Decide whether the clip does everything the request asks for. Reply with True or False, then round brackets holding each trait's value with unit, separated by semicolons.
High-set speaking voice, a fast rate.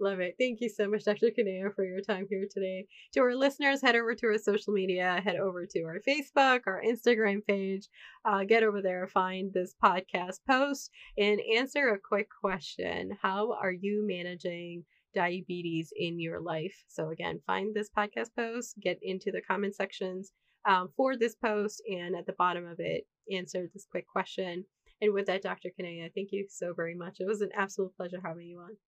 False (195 Hz; 195 wpm)